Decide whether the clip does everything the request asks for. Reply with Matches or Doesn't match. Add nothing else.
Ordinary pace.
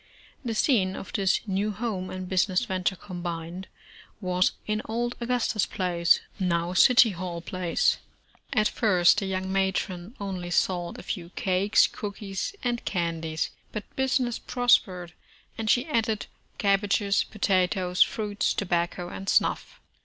Doesn't match